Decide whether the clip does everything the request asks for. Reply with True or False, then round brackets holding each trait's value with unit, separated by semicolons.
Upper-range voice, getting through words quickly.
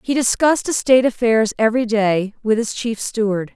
False (230 Hz; 170 wpm)